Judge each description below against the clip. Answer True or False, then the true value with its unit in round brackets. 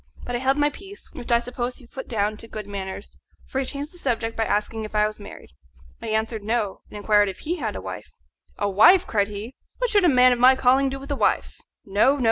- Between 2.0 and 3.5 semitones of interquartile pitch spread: False (4.3 semitones)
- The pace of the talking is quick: True (255 wpm)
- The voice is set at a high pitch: True (235 Hz)